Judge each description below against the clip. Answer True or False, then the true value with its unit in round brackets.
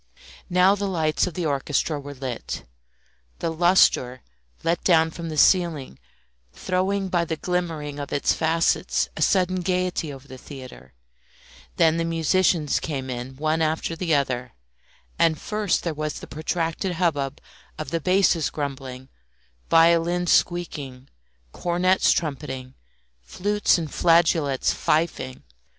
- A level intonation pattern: False (3.7 semitones)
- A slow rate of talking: True (130 wpm)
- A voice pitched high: False (160 Hz)